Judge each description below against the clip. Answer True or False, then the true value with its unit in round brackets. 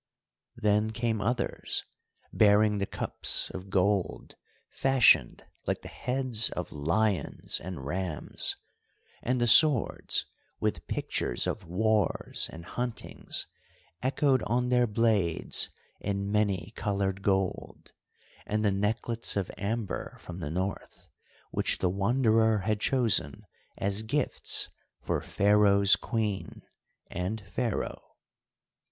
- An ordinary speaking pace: False (110 wpm)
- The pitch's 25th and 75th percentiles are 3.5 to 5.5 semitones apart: False (2.9 semitones)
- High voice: False (105 Hz)